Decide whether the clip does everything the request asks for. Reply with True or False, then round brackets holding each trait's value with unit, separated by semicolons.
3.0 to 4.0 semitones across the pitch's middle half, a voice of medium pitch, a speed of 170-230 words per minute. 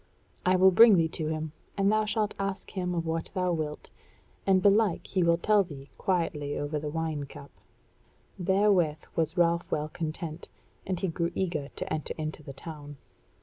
True (3.6 semitones; 170 Hz; 180 wpm)